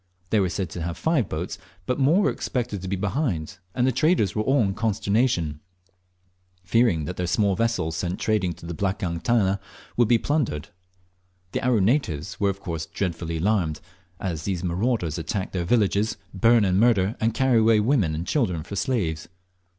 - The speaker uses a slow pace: No, average, 180 wpm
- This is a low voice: Yes, low, 100 Hz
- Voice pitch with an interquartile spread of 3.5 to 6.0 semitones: Yes, average, 5.2 semitones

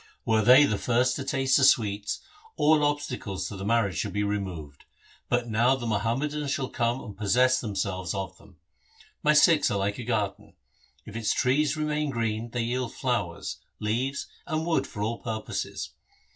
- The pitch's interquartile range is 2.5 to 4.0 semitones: No, average, 4.6 semitones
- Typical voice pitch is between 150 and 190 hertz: No, low, 115 Hz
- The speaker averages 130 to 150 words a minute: No, average, 175 wpm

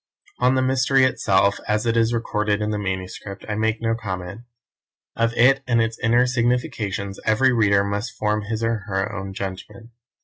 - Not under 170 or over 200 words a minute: Yes, average, 175 wpm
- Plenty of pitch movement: No, average, 2.8 semitones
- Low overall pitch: Yes, low, 110 Hz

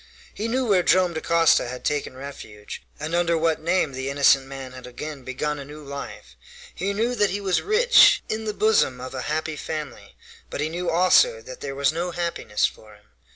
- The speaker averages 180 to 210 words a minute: Yes, average, 200 wpm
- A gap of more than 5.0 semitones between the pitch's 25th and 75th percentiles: Yes, wide, 5.4 semitones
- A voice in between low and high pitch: Yes, medium, 155 Hz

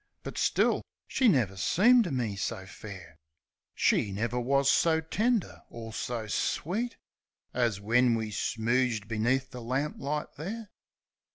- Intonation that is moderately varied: No, wide, 6.2 semitones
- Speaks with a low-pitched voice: Yes, low, 125 Hz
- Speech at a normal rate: No, slow, 130 wpm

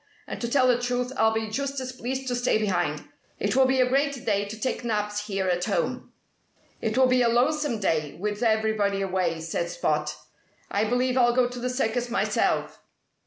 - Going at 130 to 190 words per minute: No, average, 200 wpm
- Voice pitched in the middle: No, high, 230 Hz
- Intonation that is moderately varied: Yes, average, 3.9 semitones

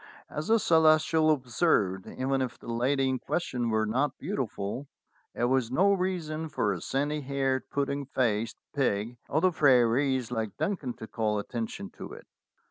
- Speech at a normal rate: Yes, average, 160 wpm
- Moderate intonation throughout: Yes, average, 4.8 semitones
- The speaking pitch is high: No, low, 130 Hz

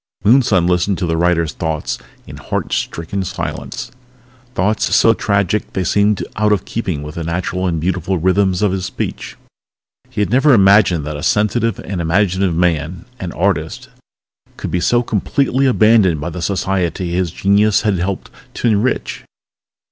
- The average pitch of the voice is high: No, very low, 95 Hz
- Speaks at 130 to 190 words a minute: Yes, average, 160 wpm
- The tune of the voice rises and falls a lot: No, average, 3.3 semitones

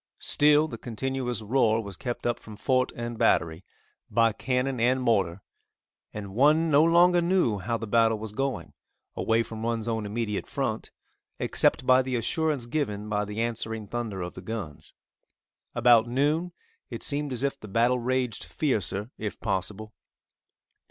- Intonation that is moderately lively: Yes, average, 3.6 semitones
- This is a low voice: Yes, low, 115 Hz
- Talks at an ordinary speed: Yes, average, 160 wpm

